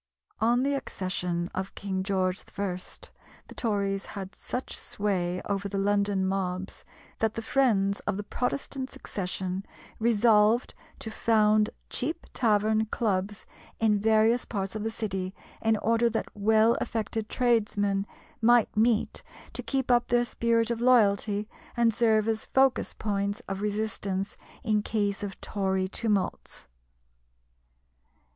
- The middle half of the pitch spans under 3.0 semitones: Yes, narrow, 2.6 semitones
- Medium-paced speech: No, slow, 130 wpm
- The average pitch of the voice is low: No, high, 210 Hz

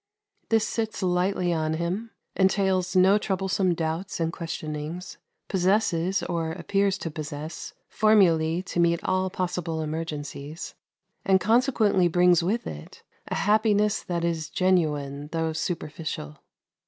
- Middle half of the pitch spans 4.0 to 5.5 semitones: No, average, 3.2 semitones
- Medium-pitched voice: Yes, medium, 175 Hz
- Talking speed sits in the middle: No, slow, 120 wpm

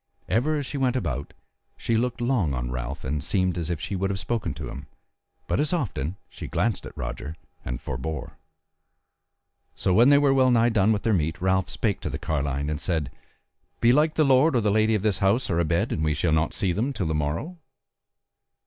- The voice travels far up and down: Yes, wide, 7.7 semitones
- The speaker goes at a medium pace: No, fast, 210 wpm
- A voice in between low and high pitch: No, very low, 95 Hz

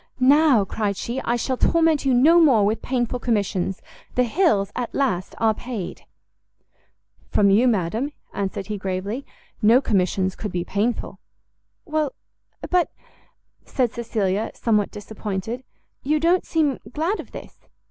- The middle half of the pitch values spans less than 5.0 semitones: No, wide, 5.4 semitones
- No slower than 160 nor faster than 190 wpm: No, slow, 135 wpm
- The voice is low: No, high, 230 Hz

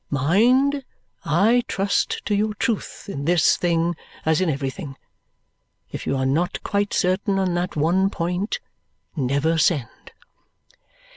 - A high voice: No, medium, 175 Hz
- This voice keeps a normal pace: No, slow, 130 wpm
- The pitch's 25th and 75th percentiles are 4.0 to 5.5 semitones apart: Yes, average, 4.6 semitones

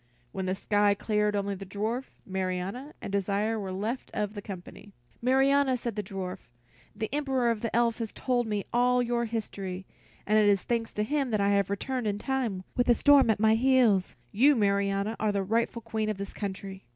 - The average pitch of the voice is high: Yes, high, 215 Hz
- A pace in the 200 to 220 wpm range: Yes, fast, 205 wpm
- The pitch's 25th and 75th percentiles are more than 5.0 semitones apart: No, average, 3.3 semitones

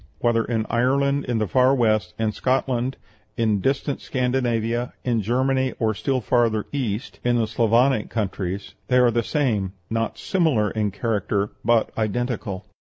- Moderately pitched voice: No, low, 120 Hz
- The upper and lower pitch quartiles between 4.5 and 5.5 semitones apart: No, average, 2.9 semitones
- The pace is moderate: Yes, average, 150 wpm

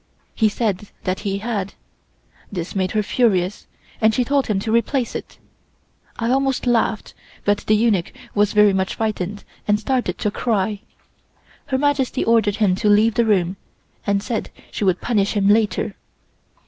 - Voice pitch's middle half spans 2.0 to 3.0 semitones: Yes, average, 2.7 semitones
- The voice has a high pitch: Yes, high, 210 Hz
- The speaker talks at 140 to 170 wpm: Yes, average, 160 wpm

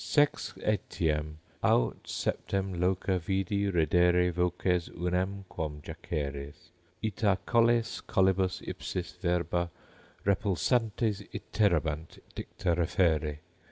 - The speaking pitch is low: Yes, very low, 90 Hz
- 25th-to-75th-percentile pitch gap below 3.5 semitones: Yes, average, 2.9 semitones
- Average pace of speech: No, slow, 85 wpm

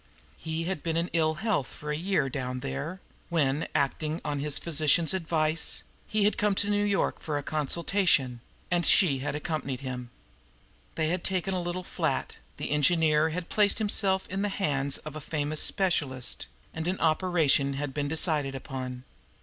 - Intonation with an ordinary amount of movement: Yes, average, 4.2 semitones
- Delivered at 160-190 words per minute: Yes, average, 170 wpm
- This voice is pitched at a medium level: Yes, medium, 155 Hz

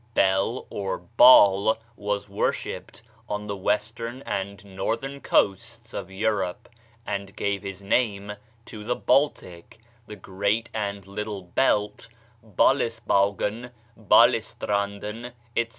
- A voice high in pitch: No, low, 105 Hz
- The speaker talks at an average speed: No, slow, 105 wpm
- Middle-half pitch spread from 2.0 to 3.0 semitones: Yes, narrow, 2.5 semitones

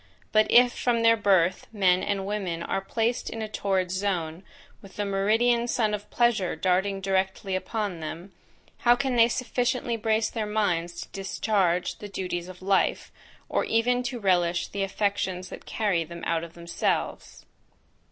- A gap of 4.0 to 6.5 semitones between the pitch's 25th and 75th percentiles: No, average, 3.6 semitones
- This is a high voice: Yes, high, 200 Hz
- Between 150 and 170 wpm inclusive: Yes, average, 160 wpm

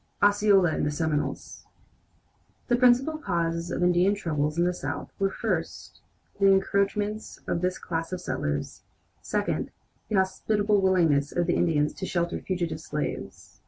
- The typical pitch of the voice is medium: Yes, medium, 180 Hz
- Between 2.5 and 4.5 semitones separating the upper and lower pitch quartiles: Yes, average, 3.4 semitones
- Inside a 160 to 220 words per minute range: No, average, 145 wpm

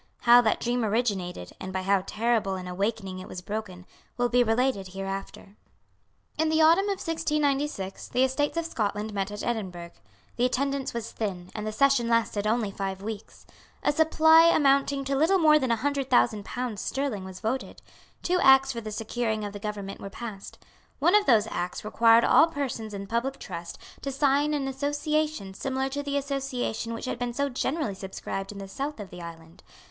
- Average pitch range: No, wide, 5.8 semitones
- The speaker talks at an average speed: Yes, average, 190 wpm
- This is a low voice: No, high, 235 Hz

